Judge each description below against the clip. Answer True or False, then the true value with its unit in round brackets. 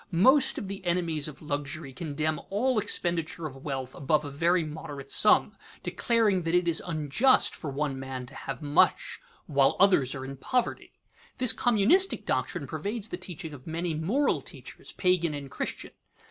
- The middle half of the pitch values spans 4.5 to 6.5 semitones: True (5.5 semitones)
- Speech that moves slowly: False (165 wpm)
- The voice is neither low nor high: True (165 Hz)